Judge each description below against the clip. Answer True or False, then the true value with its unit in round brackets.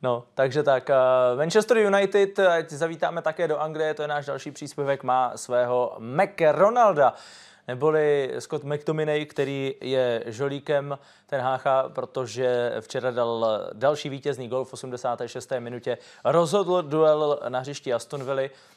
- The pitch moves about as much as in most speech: True (3.2 semitones)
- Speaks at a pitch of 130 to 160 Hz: True (140 Hz)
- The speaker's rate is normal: True (130 wpm)